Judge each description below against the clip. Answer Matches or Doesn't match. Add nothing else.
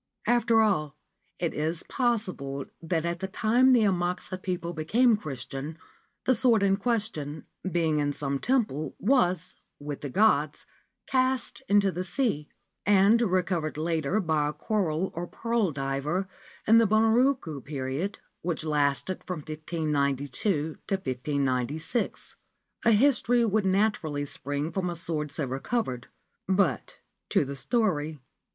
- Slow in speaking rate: Matches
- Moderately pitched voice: Matches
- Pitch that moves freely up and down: Matches